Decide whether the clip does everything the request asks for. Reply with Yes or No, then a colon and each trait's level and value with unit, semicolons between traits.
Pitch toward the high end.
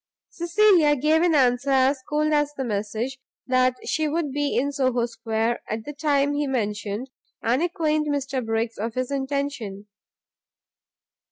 Yes: very high, 270 Hz